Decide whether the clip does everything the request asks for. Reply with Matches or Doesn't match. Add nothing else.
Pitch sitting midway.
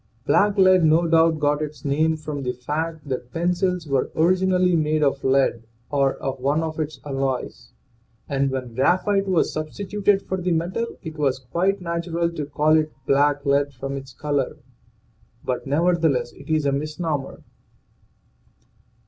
Matches